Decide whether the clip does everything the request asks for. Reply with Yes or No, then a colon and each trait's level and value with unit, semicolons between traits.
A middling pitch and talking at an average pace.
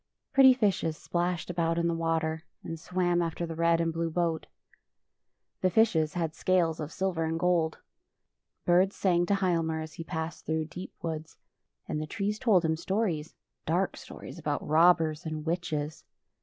Yes: medium, 165 Hz; average, 170 wpm